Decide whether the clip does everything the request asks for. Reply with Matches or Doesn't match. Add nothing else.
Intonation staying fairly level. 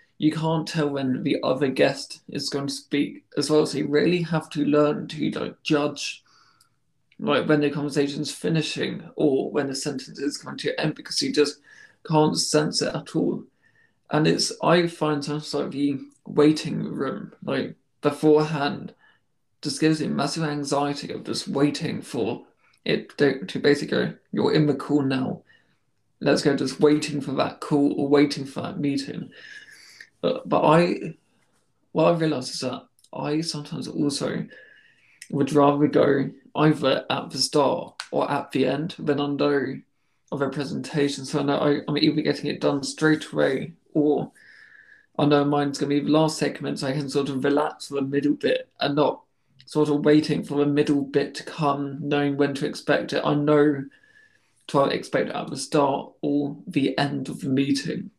Matches